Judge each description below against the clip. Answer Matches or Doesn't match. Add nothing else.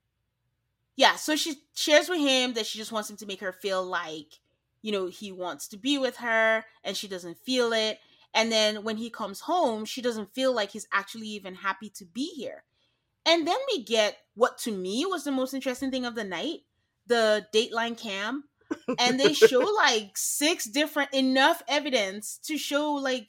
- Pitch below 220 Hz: Doesn't match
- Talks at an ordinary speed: Matches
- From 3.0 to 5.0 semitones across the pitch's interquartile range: Doesn't match